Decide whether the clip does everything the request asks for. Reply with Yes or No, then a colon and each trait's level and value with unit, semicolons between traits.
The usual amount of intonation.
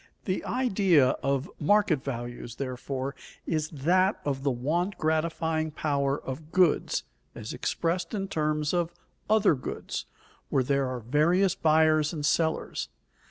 Yes: average, 4.0 semitones